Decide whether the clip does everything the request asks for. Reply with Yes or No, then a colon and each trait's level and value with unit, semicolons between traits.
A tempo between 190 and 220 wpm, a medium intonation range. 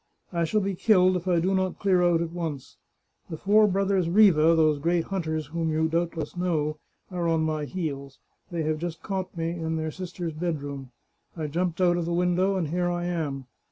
No: average, 200 wpm; narrow, 2.3 semitones